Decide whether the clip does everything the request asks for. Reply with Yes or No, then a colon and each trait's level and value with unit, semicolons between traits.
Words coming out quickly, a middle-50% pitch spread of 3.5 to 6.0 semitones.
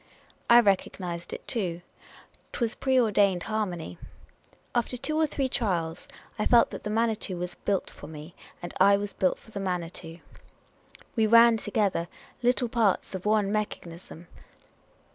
No: average, 155 wpm; average, 4.5 semitones